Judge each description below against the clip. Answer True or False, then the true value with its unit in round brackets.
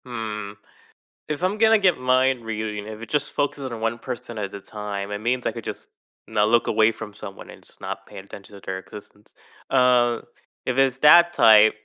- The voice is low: True (115 Hz)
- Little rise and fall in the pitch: False (3.4 semitones)